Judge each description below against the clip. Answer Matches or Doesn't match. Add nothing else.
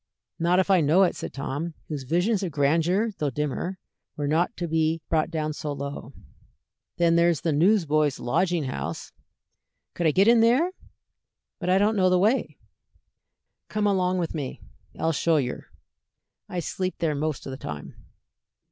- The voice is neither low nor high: Matches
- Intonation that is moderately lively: Matches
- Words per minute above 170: Doesn't match